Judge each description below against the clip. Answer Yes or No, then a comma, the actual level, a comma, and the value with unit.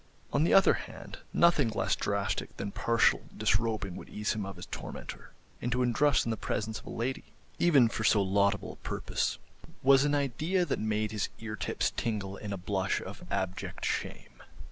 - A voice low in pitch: Yes, low, 110 Hz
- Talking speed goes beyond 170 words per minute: Yes, average, 185 wpm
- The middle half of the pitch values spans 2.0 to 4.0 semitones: No, average, 4.7 semitones